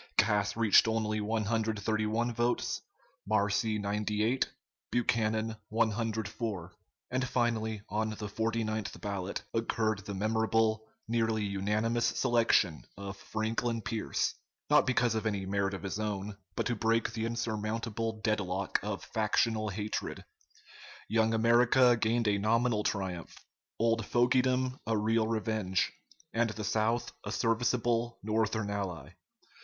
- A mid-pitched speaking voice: No, low, 110 Hz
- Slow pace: Yes, slow, 120 wpm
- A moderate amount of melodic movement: No, narrow, 1.7 semitones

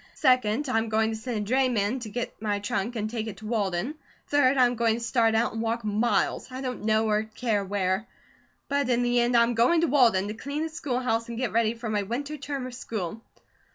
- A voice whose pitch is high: Yes, high, 230 Hz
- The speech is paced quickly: Yes, fast, 225 wpm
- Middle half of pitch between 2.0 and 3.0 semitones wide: Yes, average, 2.7 semitones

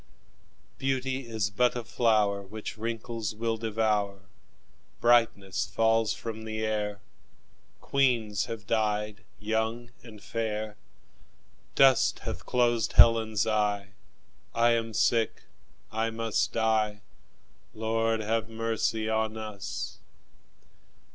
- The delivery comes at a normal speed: No, slow, 100 wpm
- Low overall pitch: Yes, low, 110 Hz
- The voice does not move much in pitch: Yes, narrow, 1.3 semitones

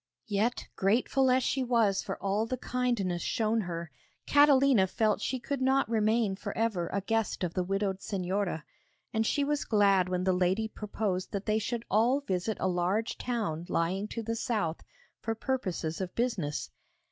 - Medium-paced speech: Yes, average, 170 wpm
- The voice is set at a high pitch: Yes, high, 210 Hz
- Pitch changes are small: No, average, 4.2 semitones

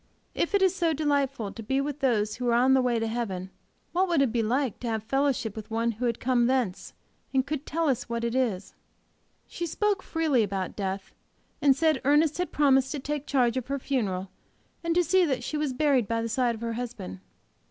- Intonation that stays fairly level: No, average, 4.3 semitones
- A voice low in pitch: No, very high, 255 Hz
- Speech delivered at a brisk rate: Yes, fast, 220 wpm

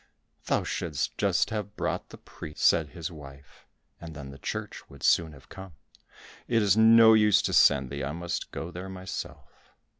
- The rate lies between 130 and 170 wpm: No, average, 180 wpm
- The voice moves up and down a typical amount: No, wide, 5.8 semitones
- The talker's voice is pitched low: Yes, very low, 85 Hz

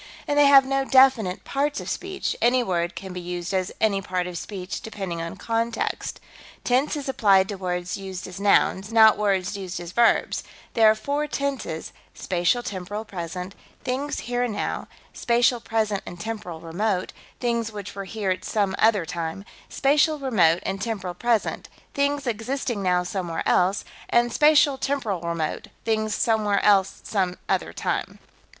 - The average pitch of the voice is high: Yes, high, 210 Hz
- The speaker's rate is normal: Yes, average, 165 wpm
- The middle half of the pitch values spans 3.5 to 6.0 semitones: Yes, average, 4.9 semitones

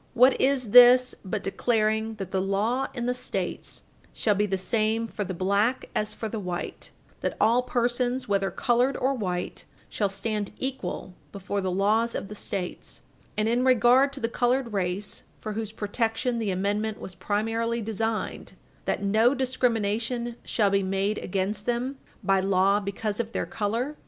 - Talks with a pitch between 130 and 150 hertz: No, high, 220 Hz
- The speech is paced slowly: No, average, 165 wpm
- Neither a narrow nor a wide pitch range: Yes, average, 3.3 semitones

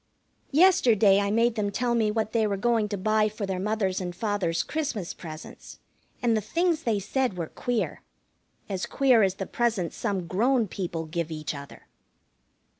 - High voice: Yes, high, 210 Hz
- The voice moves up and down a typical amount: Yes, average, 4.0 semitones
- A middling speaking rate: Yes, average, 175 wpm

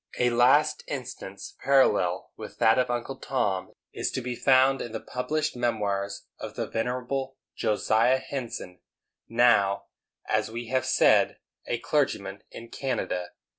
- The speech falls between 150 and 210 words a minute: No, slow, 135 wpm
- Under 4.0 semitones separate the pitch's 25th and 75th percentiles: Yes, average, 3.6 semitones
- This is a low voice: Yes, low, 120 Hz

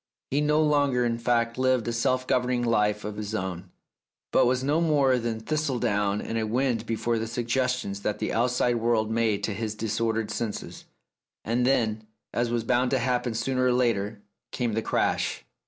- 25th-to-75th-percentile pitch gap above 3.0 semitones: No, narrow, 2.6 semitones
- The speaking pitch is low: Yes, low, 115 Hz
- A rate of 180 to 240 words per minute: Yes, average, 190 wpm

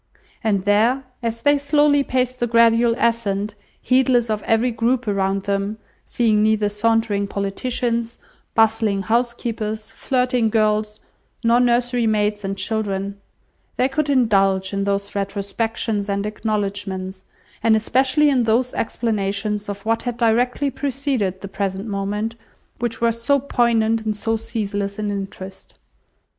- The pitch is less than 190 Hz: No, high, 220 Hz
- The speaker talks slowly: Yes, slow, 130 wpm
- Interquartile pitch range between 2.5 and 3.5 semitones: Yes, average, 2.9 semitones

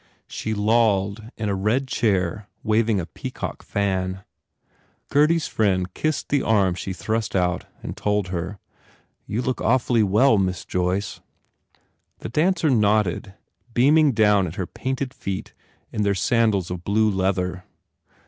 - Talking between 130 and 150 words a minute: Yes, average, 140 wpm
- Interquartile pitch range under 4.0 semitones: Yes, average, 3.6 semitones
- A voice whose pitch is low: Yes, low, 105 Hz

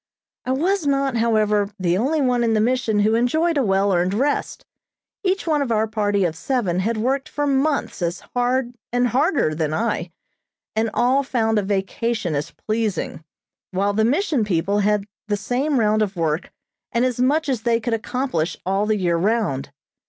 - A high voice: Yes, high, 225 Hz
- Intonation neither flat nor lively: Yes, average, 4.5 semitones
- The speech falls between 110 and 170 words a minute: No, average, 180 wpm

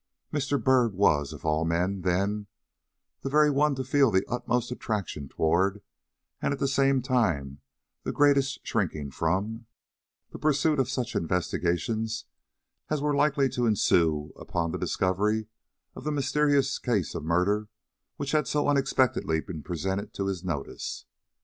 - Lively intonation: Yes, wide, 7.3 semitones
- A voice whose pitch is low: Yes, low, 110 Hz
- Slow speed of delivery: No, average, 150 wpm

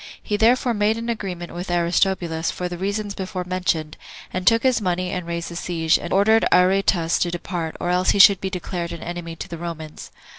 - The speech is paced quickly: Yes, fast, 210 wpm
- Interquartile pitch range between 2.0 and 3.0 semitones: Yes, narrow, 2.6 semitones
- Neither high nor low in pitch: Yes, medium, 180 Hz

